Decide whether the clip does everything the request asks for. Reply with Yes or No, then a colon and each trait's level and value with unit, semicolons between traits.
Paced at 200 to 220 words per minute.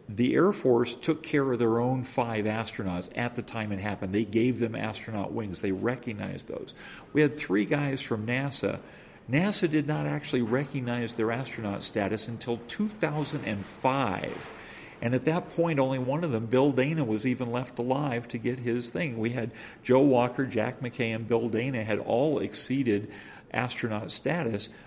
No: average, 175 wpm